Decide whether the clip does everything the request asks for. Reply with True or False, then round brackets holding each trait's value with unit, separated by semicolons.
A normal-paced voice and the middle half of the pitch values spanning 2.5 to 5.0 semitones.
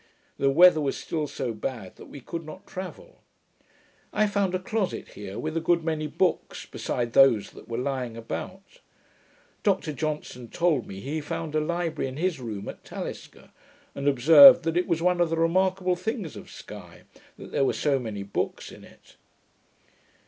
False (180 wpm; 5.5 semitones)